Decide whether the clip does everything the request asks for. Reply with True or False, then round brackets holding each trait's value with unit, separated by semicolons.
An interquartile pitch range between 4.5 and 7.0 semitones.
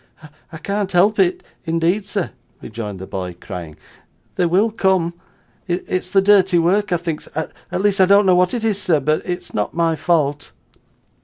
False (3.6 semitones)